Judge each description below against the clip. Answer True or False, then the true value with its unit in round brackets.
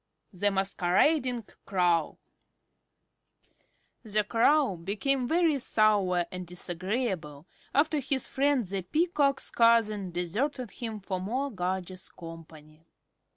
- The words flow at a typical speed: False (100 wpm)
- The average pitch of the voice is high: True (205 Hz)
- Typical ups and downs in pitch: False (6.4 semitones)